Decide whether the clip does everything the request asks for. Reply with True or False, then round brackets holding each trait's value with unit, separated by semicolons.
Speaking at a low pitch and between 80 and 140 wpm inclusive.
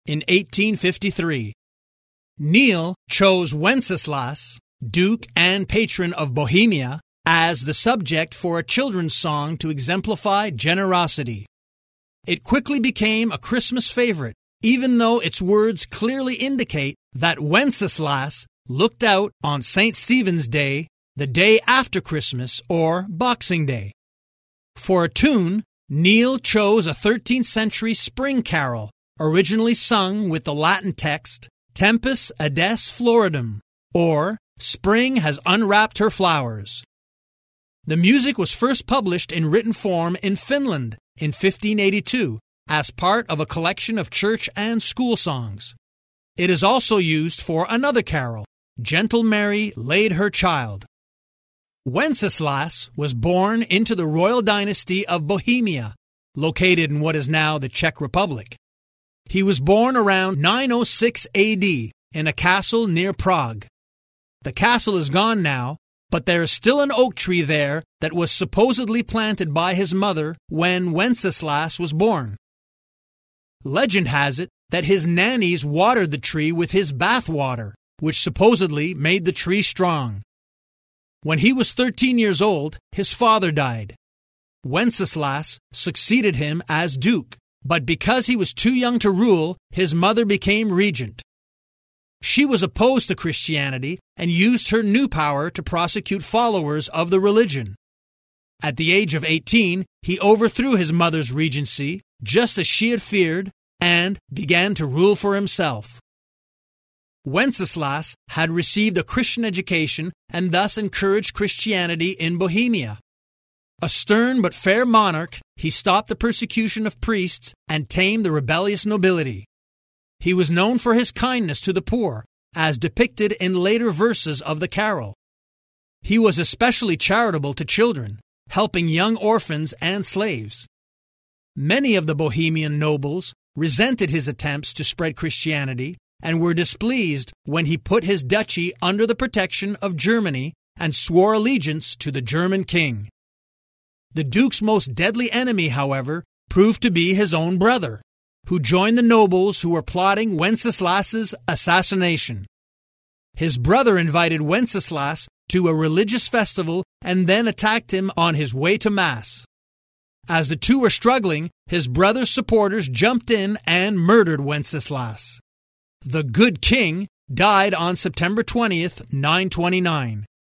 False (180 Hz; 135 wpm)